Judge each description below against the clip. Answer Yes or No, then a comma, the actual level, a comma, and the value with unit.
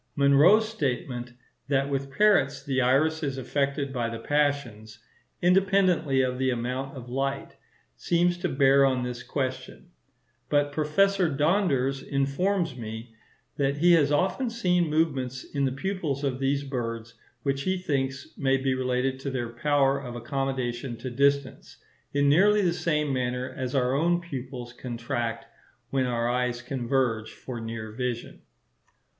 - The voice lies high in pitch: No, low, 135 Hz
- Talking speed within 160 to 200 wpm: No, average, 145 wpm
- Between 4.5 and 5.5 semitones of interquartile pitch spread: No, average, 3.0 semitones